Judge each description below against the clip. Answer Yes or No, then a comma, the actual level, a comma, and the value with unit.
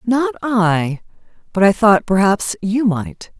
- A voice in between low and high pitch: No, high, 205 Hz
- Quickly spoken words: No, average, 140 wpm